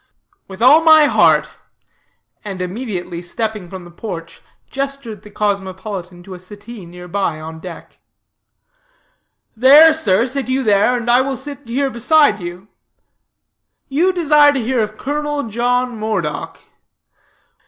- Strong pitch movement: Yes, wide, 6.4 semitones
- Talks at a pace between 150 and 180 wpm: No, slow, 135 wpm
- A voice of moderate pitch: No, high, 220 Hz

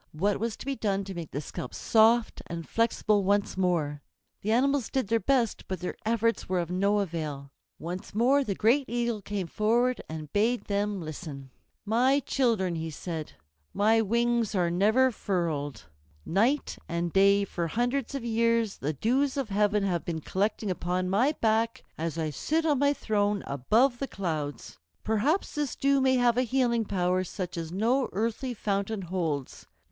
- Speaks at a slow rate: No, average, 170 wpm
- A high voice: Yes, high, 205 Hz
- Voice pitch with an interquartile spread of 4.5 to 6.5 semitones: Yes, average, 5.1 semitones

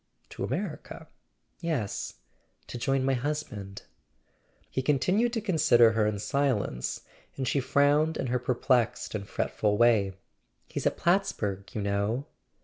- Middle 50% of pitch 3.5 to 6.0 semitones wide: Yes, wide, 5.6 semitones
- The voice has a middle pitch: No, low, 125 Hz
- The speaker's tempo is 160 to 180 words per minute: No, slow, 135 wpm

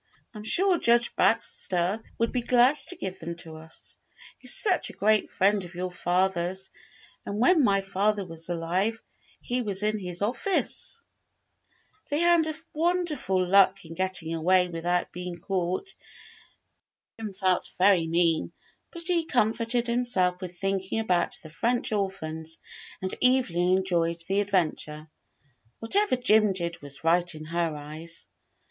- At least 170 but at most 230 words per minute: No, average, 140 wpm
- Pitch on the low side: No, high, 190 Hz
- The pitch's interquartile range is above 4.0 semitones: Yes, average, 4.8 semitones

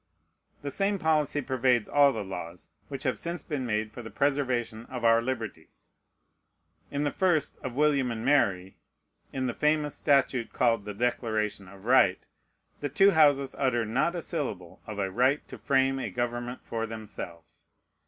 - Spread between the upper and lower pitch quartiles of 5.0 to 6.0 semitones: No, average, 4.5 semitones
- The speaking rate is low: No, average, 165 wpm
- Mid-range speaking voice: No, low, 125 Hz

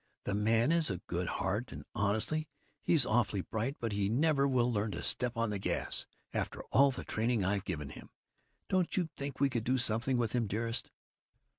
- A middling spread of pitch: Yes, average, 4.3 semitones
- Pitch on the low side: Yes, low, 115 Hz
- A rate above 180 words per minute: Yes, average, 195 wpm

